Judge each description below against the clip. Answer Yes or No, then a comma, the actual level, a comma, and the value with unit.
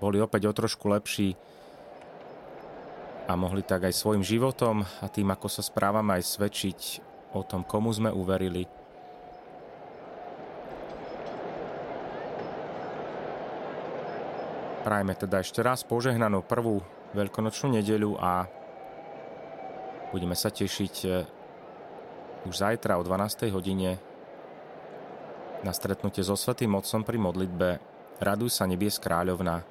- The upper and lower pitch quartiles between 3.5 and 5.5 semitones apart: No, average, 2.7 semitones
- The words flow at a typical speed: No, slow, 105 wpm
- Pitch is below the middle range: Yes, low, 100 Hz